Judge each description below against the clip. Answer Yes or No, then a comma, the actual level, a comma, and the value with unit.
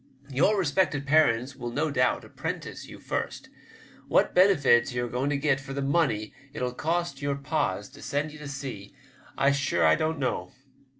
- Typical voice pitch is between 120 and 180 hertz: Yes, medium, 140 Hz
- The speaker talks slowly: No, average, 180 wpm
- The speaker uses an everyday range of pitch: Yes, average, 3.4 semitones